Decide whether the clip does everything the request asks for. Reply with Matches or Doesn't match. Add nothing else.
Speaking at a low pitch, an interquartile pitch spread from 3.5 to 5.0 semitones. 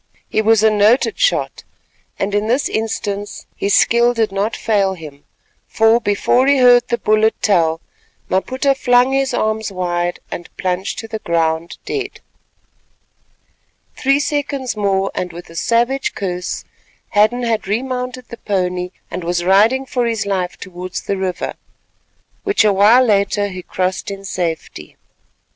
Doesn't match